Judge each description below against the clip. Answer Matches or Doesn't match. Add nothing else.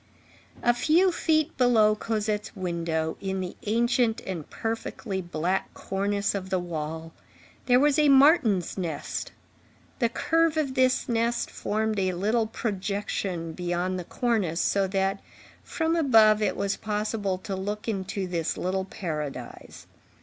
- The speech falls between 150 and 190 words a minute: Doesn't match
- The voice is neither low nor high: Doesn't match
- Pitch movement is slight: Doesn't match